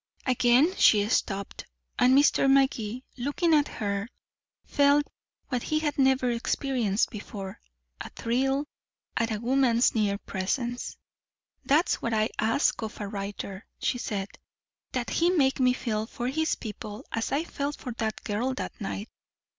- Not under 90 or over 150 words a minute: Yes, average, 145 wpm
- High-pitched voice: Yes, high, 245 Hz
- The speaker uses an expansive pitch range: No, average, 4.3 semitones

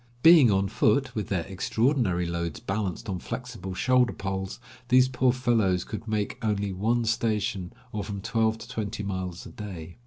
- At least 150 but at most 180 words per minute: Yes, average, 165 wpm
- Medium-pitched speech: No, low, 105 Hz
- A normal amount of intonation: Yes, average, 3.8 semitones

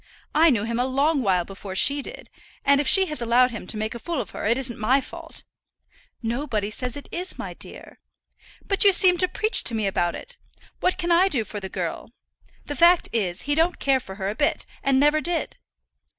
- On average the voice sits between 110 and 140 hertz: No, very high, 265 Hz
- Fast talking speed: Yes, fast, 220 wpm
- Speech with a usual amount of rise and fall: No, wide, 7.0 semitones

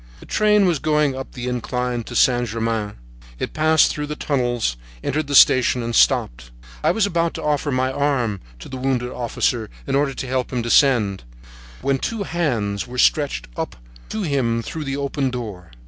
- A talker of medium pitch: No, low, 130 Hz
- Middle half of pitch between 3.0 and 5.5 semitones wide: Yes, average, 3.9 semitones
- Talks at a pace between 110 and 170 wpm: No, average, 185 wpm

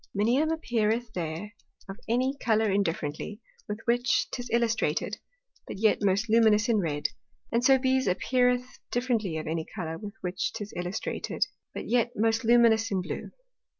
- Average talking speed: Yes, average, 150 wpm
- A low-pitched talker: No, high, 220 Hz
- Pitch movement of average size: Yes, average, 3.8 semitones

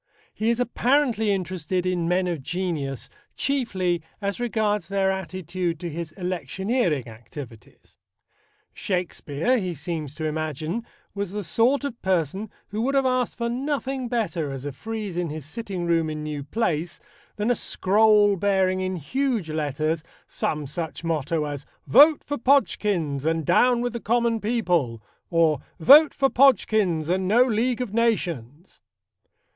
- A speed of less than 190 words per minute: Yes, average, 150 wpm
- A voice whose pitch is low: No, medium, 185 Hz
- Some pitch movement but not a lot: No, wide, 6.4 semitones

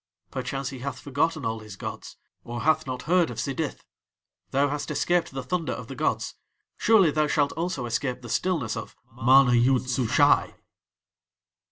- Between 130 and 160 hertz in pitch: Yes, low, 135 Hz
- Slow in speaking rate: No, average, 165 wpm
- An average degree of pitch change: Yes, average, 3.9 semitones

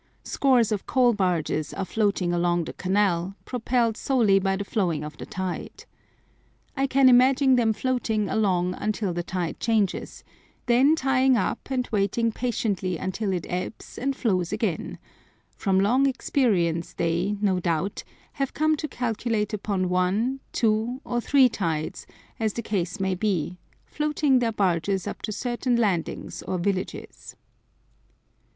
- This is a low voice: No, high, 210 Hz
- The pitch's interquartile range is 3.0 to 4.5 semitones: No, average, 5.1 semitones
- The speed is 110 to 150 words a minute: Yes, average, 145 wpm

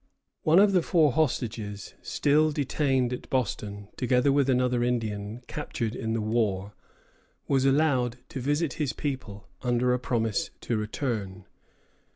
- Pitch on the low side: Yes, low, 125 Hz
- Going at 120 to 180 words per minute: Yes, average, 140 wpm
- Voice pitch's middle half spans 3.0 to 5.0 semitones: Yes, average, 4.4 semitones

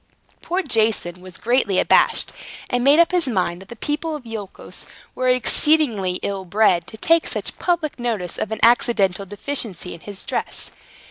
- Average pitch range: No, wide, 6.6 semitones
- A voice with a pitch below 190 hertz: No, high, 225 Hz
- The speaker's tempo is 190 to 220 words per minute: No, average, 165 wpm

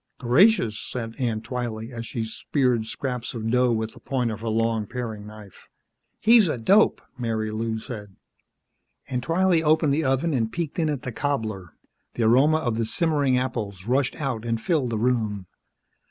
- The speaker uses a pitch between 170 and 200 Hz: No, low, 120 Hz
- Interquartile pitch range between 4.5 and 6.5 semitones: No, average, 3.9 semitones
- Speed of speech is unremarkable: Yes, average, 170 wpm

